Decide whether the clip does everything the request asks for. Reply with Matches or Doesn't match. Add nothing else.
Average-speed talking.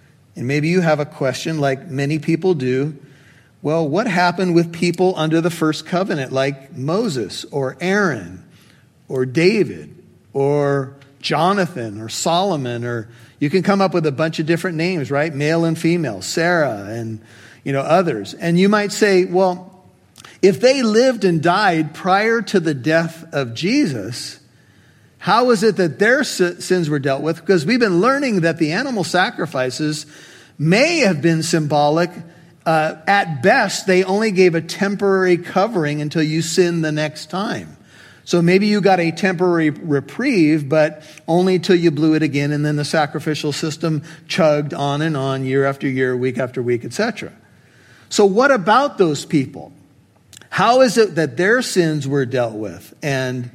Matches